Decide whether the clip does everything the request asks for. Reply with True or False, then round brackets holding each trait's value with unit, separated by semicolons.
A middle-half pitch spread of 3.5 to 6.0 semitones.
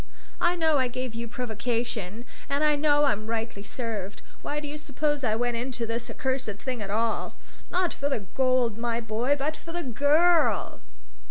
True (4.2 semitones)